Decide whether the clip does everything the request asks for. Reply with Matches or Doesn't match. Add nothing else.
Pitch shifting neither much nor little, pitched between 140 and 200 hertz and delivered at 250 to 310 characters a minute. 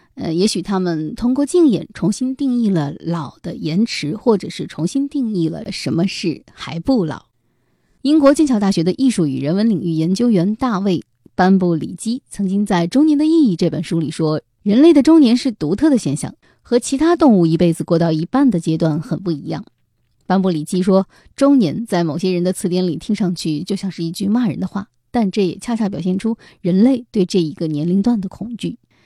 Doesn't match